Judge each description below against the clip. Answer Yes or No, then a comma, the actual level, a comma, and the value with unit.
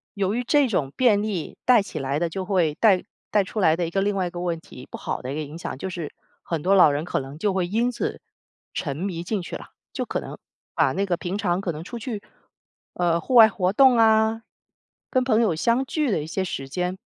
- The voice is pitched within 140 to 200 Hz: Yes, medium, 185 Hz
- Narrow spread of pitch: No, average, 4.7 semitones